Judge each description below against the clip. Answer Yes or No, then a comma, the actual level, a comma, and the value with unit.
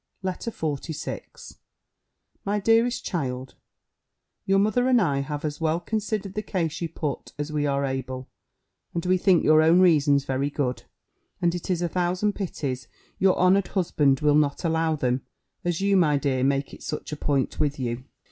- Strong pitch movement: No, average, 4.8 semitones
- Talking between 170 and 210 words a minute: Yes, average, 175 wpm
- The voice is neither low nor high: Yes, medium, 160 Hz